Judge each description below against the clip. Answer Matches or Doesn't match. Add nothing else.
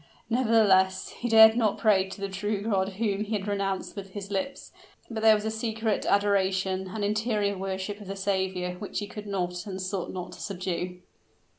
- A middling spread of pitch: Doesn't match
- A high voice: Matches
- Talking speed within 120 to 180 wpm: Doesn't match